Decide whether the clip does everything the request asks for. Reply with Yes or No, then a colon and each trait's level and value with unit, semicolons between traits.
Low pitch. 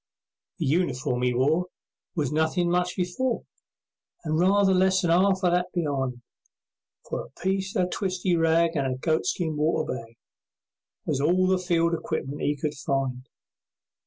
No: medium, 165 Hz